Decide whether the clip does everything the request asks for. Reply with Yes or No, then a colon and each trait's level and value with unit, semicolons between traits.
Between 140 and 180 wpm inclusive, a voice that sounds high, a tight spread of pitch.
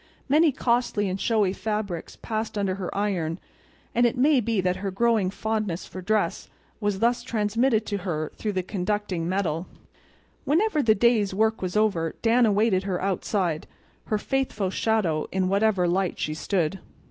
No: average, 160 wpm; high, 205 Hz; average, 3.2 semitones